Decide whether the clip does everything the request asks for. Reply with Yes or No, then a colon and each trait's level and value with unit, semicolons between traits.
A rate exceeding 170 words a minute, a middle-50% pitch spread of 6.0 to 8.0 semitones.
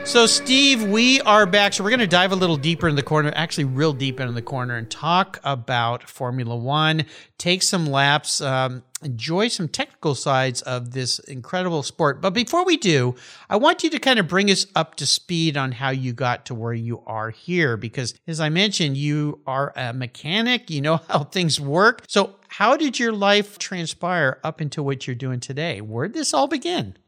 Yes: fast, 205 wpm; wide, 6.9 semitones